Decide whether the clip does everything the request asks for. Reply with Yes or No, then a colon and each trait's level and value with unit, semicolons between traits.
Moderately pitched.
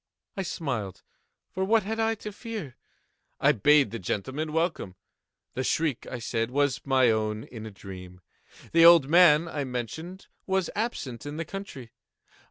Yes: medium, 145 Hz